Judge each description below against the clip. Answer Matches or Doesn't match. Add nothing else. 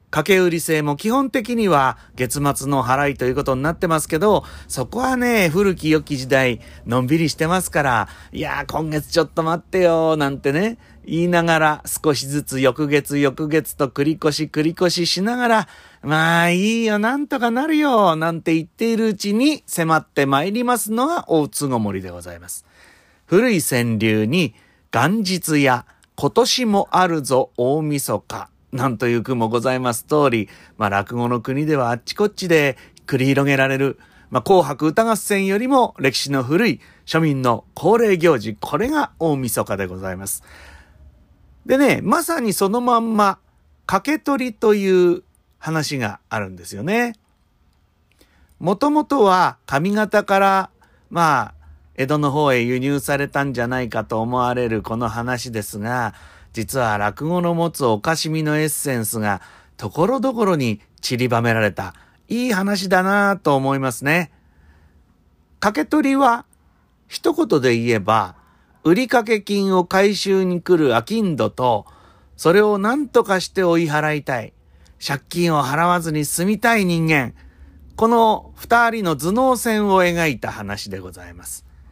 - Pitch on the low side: Doesn't match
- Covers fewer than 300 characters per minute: Matches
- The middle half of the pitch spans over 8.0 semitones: Matches